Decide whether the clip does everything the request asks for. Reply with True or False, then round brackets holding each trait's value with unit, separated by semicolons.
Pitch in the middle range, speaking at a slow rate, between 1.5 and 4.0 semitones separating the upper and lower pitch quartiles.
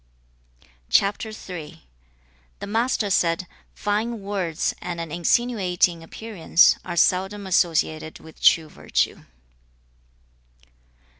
True (180 Hz; 80 wpm; 3.7 semitones)